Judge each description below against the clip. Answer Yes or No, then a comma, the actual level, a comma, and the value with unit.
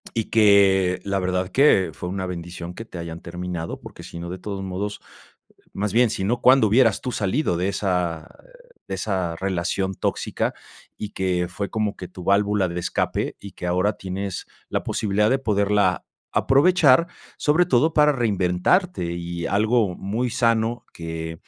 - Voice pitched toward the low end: Yes, low, 100 Hz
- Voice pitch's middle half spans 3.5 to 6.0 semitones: Yes, average, 4.1 semitones